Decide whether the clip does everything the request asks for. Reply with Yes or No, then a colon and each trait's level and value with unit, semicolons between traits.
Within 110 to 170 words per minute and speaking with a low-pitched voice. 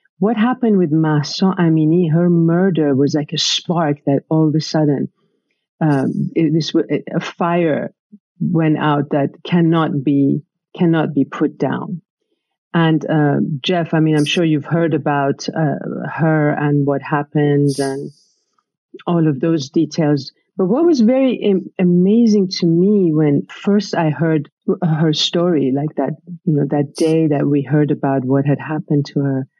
No: average, 160 wpm; medium, 160 Hz